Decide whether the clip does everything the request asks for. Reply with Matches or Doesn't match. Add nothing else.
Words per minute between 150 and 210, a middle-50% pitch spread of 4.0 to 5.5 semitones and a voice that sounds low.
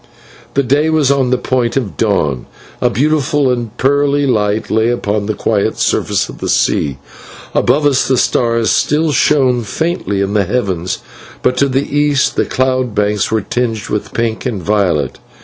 Matches